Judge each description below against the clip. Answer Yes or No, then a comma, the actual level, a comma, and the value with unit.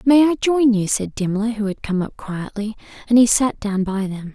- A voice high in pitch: Yes, high, 220 Hz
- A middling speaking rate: No, fast, 235 wpm